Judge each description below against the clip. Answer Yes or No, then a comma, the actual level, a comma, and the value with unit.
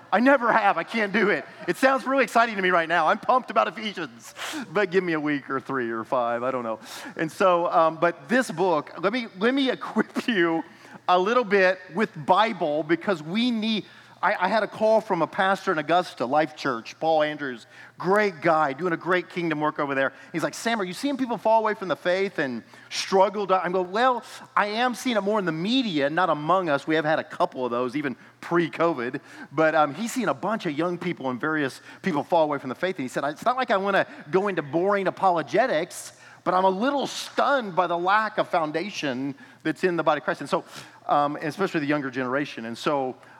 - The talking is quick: Yes, fast, 230 wpm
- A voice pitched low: No, medium, 180 Hz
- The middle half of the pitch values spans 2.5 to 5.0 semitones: No, wide, 5.4 semitones